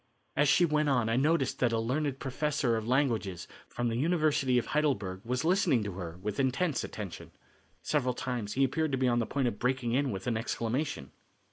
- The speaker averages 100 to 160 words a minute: No, fast, 205 wpm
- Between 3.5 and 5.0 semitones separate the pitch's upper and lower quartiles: Yes, average, 4.1 semitones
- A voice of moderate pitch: No, low, 125 Hz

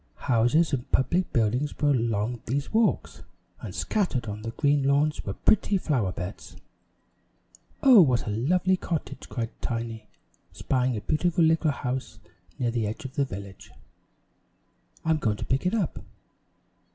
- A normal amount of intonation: No, wide, 5.8 semitones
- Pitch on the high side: No, low, 130 Hz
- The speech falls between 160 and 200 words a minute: No, average, 150 wpm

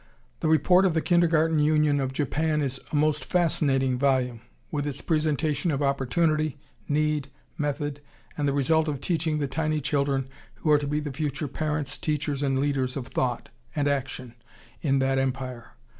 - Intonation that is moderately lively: No, narrow, 2.3 semitones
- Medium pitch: Yes, medium, 145 Hz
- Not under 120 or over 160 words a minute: No, average, 170 wpm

